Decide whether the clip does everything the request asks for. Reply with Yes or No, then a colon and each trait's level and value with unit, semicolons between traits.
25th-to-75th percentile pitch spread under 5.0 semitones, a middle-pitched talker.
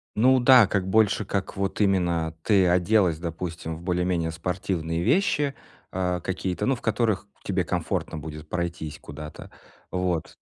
No: average, 3.2 semitones; very low, 90 Hz